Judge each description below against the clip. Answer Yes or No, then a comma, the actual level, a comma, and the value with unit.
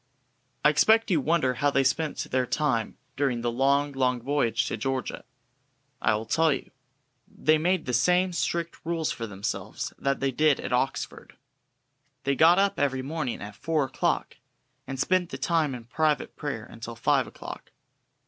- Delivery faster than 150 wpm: Yes, average, 165 wpm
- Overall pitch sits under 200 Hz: Yes, medium, 140 Hz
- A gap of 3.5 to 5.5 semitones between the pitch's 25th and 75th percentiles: Yes, average, 4.2 semitones